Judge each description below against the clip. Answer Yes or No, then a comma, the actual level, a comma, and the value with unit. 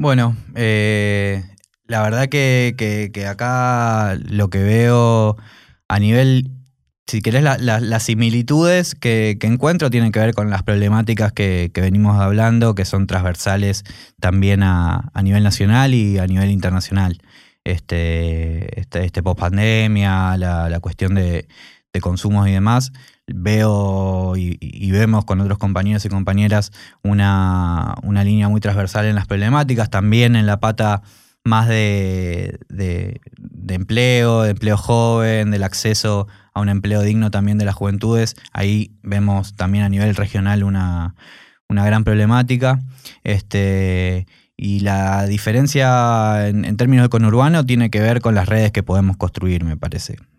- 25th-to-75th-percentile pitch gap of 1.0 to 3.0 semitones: Yes, average, 2.7 semitones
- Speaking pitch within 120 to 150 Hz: No, low, 105 Hz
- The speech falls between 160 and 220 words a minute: No, average, 150 wpm